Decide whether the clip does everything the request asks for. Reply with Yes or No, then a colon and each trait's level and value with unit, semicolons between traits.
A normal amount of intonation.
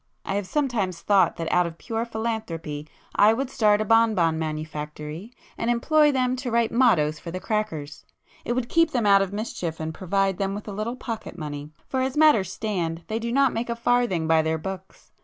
No: wide, 6.1 semitones